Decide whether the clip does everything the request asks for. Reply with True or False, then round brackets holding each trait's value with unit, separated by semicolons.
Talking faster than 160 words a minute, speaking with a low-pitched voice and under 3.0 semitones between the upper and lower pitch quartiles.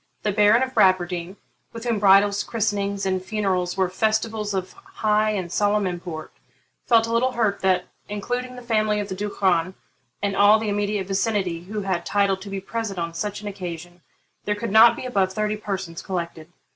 False (185 wpm; 200 Hz; 2.4 semitones)